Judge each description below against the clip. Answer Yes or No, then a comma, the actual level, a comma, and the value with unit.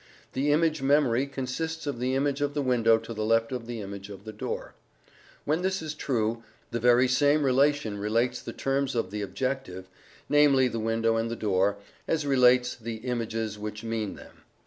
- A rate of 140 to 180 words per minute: No, average, 190 wpm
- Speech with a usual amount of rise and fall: Yes, average, 3.7 semitones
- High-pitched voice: No, low, 125 Hz